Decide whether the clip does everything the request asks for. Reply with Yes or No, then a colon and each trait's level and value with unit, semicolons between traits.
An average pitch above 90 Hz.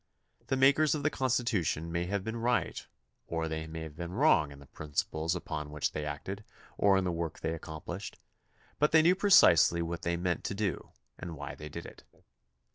No: very low, 85 Hz